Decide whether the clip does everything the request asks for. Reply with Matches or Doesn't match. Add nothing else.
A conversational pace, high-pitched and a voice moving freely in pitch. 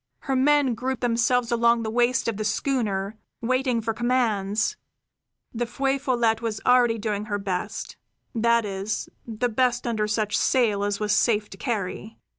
Doesn't match